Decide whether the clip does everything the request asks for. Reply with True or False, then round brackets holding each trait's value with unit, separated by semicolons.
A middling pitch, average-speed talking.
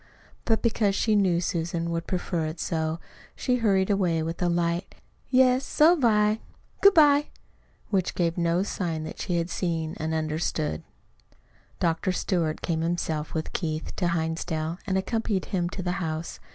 True (175 Hz; 160 wpm)